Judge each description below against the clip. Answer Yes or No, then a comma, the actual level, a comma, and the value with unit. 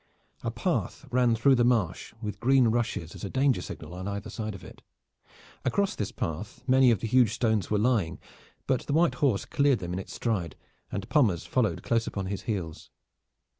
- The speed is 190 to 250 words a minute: Yes, average, 195 wpm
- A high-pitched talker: No, low, 110 Hz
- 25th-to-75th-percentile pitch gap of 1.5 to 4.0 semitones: No, average, 4.6 semitones